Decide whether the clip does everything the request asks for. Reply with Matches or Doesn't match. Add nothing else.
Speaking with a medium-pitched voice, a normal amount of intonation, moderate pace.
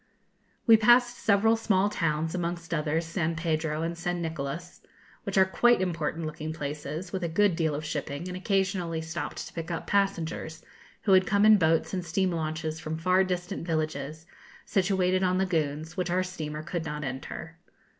Matches